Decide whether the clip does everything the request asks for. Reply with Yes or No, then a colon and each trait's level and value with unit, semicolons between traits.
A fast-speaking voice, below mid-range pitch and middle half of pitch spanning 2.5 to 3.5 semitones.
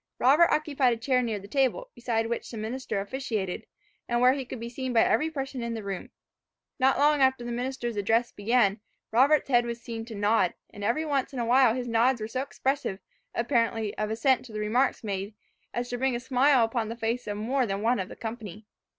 No: fast, 220 wpm; high, 240 Hz; average, 2.9 semitones